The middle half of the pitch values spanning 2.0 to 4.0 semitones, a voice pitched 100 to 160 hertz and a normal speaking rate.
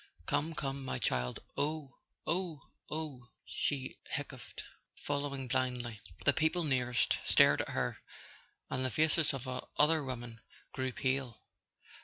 No: average, 3.2 semitones; low, 135 Hz; slow, 120 wpm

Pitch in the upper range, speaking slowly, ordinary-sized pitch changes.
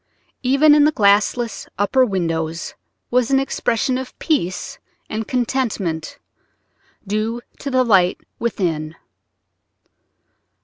No: high, 225 Hz; slow, 100 wpm; wide, 5.8 semitones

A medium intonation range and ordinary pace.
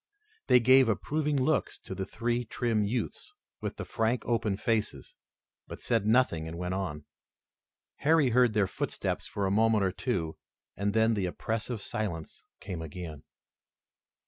Yes: average, 4.2 semitones; average, 150 wpm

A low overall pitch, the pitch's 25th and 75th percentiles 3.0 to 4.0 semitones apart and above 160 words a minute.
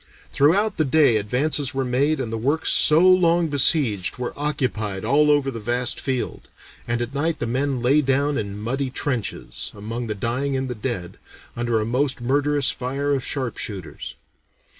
Yes: low, 130 Hz; average, 3.4 semitones; average, 170 wpm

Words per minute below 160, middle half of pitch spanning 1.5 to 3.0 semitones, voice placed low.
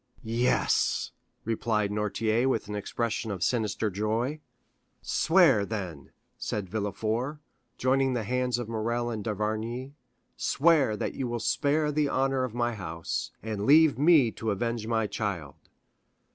No: slow, 135 wpm; average, 3.4 semitones; low, 115 Hz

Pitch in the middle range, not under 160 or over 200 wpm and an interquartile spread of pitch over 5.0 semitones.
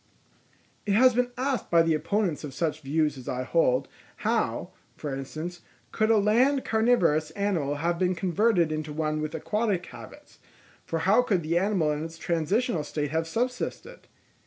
Yes: medium, 170 Hz; average, 165 wpm; wide, 5.6 semitones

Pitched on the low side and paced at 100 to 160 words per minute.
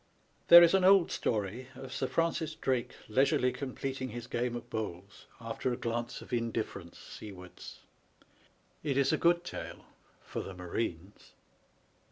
Yes: low, 120 Hz; average, 145 wpm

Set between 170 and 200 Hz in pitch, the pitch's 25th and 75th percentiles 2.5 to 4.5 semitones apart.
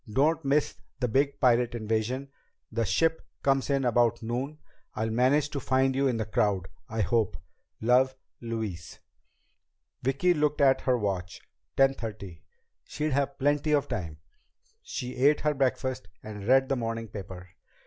No: low, 125 Hz; average, 4.0 semitones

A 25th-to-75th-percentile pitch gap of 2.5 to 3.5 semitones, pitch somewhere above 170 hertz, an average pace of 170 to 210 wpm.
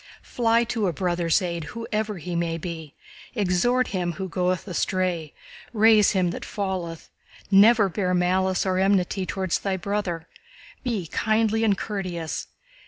No: average, 3.2 semitones; medium, 185 Hz; average, 140 wpm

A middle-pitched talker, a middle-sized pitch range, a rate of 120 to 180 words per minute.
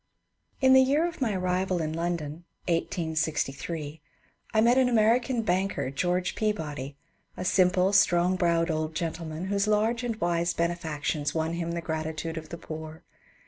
Yes: medium, 175 Hz; average, 4.1 semitones; average, 155 wpm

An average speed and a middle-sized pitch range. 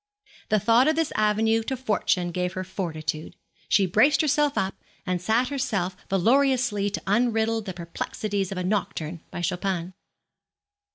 Yes: average, 150 wpm; average, 4.4 semitones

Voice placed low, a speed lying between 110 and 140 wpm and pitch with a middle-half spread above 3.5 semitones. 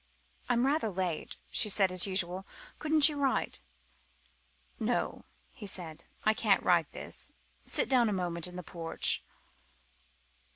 No: high, 190 Hz; slow, 135 wpm; average, 5.2 semitones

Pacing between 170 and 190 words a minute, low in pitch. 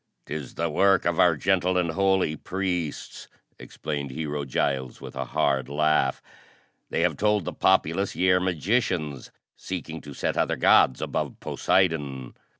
No: average, 150 wpm; very low, 80 Hz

